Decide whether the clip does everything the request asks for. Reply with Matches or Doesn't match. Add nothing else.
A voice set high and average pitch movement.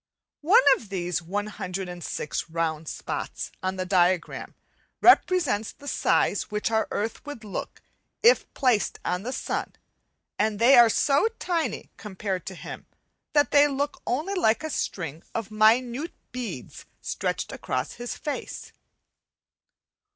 Doesn't match